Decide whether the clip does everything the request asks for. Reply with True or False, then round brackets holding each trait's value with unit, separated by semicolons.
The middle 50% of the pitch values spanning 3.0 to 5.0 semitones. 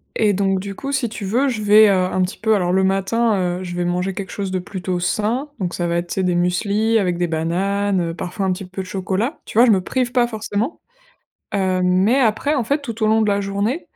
True (3.3 semitones)